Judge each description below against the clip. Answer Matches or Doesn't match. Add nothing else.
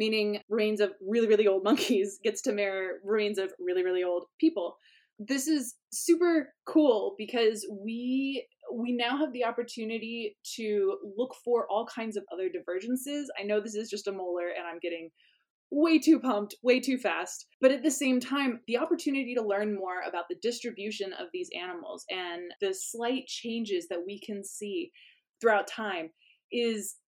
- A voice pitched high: Matches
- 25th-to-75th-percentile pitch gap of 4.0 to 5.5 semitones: Matches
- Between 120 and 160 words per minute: Doesn't match